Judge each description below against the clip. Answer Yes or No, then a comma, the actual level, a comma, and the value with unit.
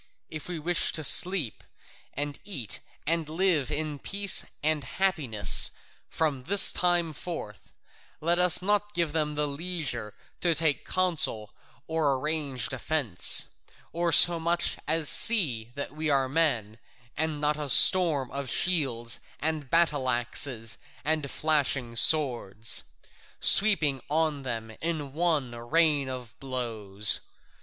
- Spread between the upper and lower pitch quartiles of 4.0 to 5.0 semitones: Yes, average, 4.4 semitones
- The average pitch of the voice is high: No, medium, 150 Hz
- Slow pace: Yes, slow, 125 wpm